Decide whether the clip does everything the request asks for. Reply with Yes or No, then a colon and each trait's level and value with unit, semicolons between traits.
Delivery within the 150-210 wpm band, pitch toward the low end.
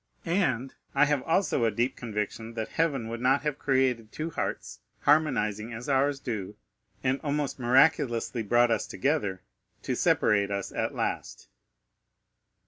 No: average, 140 wpm; low, 125 Hz